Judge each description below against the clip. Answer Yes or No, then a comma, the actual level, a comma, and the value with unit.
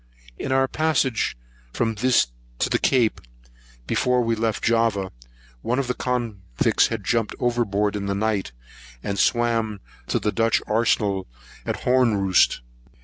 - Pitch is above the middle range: No, low, 115 Hz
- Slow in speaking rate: No, average, 145 wpm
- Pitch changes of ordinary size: Yes, average, 3.1 semitones